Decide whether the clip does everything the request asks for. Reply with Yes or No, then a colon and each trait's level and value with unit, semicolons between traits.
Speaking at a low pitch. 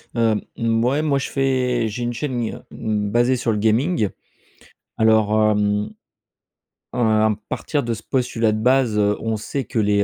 Yes: low, 115 Hz